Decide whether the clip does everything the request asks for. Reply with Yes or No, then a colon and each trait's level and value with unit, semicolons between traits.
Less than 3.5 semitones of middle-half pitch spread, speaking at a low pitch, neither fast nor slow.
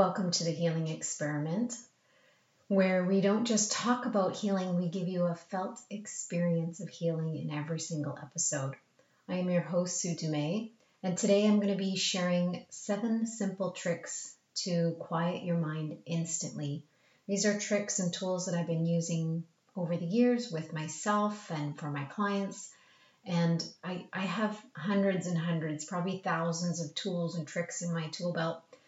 No: average, 3.0 semitones; medium, 175 Hz; average, 165 wpm